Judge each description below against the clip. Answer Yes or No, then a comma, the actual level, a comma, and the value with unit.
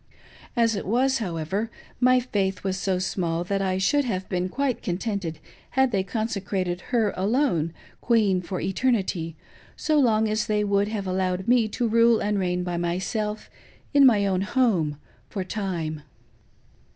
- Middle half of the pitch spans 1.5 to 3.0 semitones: No, average, 3.9 semitones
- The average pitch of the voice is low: No, high, 200 Hz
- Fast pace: No, average, 155 wpm